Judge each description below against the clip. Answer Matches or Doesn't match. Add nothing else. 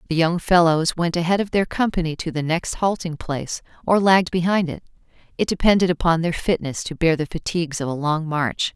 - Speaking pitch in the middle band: Matches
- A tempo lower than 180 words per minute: Doesn't match